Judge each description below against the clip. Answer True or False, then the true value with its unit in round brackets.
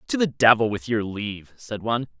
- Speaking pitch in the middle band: False (110 Hz)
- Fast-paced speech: True (220 wpm)